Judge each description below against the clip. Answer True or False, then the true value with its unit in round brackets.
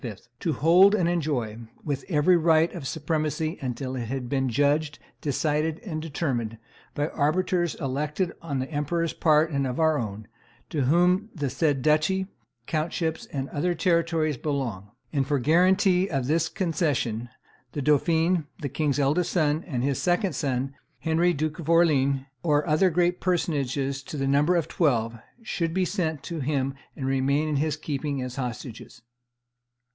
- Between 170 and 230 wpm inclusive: False (155 wpm)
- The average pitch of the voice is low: False (150 Hz)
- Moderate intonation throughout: True (3.5 semitones)